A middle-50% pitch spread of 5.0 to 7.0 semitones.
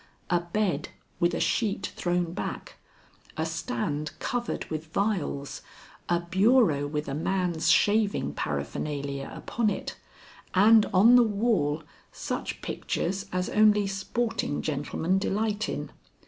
Yes: average, 5.3 semitones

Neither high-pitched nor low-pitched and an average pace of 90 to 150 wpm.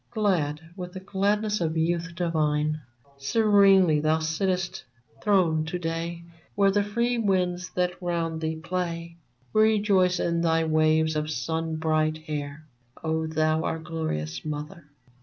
Yes: medium, 165 Hz; slow, 135 wpm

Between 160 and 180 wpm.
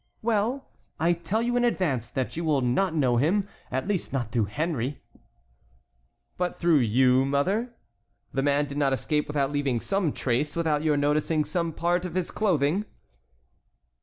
Yes: average, 165 wpm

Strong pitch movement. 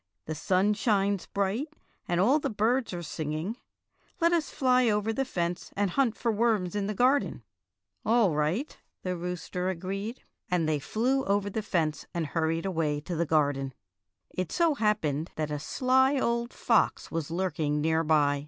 Yes: wide, 6.1 semitones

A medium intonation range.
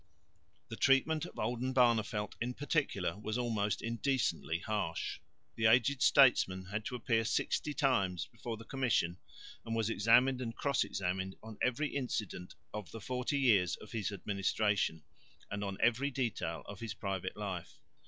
Yes: average, 4.3 semitones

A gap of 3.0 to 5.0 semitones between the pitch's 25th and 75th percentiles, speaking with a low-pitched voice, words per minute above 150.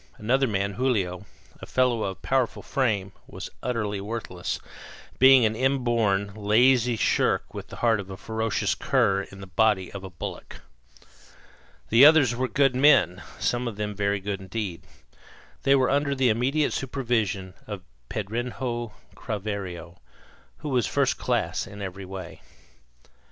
No: average, 4.4 semitones; low, 110 Hz; average, 145 wpm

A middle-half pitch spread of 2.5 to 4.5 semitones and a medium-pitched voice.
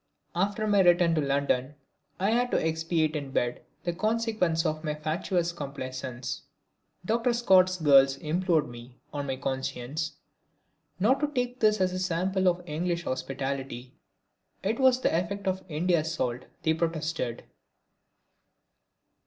No: average, 5.2 semitones; medium, 165 Hz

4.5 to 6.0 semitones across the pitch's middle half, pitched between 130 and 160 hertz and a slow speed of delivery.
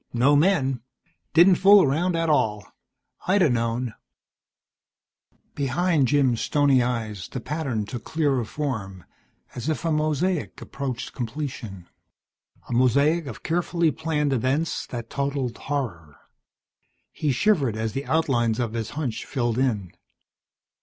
Yes: average, 4.8 semitones; low, 135 Hz; slow, 125 wpm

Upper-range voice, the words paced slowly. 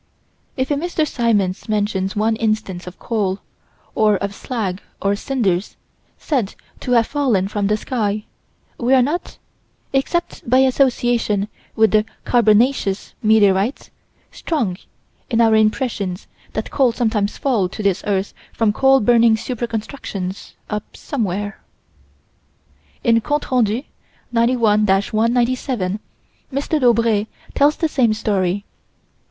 Yes: high, 220 Hz; slow, 125 wpm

